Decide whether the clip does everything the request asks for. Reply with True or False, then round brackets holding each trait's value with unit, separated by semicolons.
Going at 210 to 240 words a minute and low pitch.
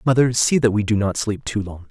False (285 wpm; 110 Hz)